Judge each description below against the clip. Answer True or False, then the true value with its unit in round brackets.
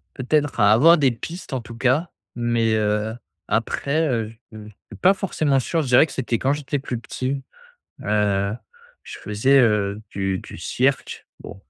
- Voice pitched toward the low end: True (125 Hz)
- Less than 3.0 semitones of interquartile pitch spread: False (4.6 semitones)